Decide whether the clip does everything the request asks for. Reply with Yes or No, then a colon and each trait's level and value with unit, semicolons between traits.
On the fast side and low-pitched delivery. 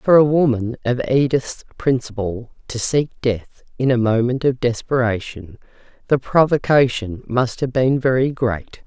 No: average, 140 wpm; low, 125 Hz